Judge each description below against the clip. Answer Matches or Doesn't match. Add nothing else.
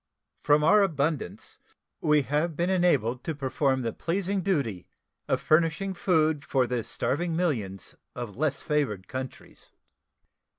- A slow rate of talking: Matches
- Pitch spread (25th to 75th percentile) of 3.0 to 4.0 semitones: Doesn't match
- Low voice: Doesn't match